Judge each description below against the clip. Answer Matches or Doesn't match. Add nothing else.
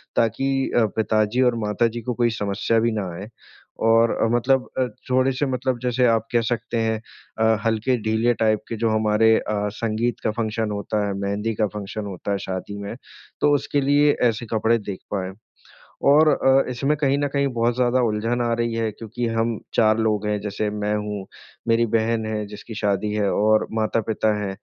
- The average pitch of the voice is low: Matches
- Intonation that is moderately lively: Doesn't match